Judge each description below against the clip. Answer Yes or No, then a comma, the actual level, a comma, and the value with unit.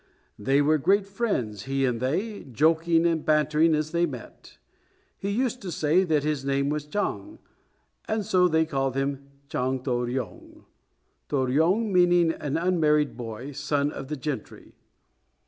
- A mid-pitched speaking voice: Yes, medium, 150 Hz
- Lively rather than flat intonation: No, average, 4.1 semitones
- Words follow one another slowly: No, average, 155 wpm